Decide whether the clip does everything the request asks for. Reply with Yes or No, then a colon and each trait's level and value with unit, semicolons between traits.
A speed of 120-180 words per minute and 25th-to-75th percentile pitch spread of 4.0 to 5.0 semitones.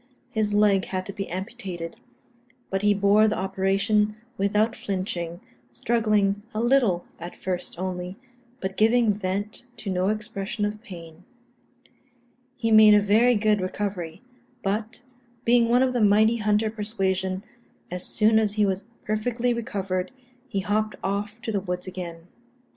No: average, 145 wpm; narrow, 2.4 semitones